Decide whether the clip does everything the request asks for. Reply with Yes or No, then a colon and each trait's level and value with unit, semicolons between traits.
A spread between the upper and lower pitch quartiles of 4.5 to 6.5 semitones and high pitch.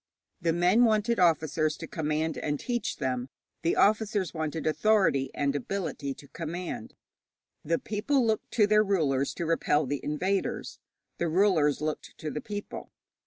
No: wide, 5.4 semitones; medium, 165 Hz